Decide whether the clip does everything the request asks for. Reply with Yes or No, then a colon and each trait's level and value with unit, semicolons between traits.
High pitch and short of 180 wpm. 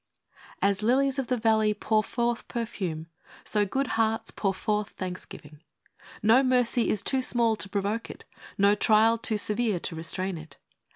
Yes: high, 215 Hz; average, 165 wpm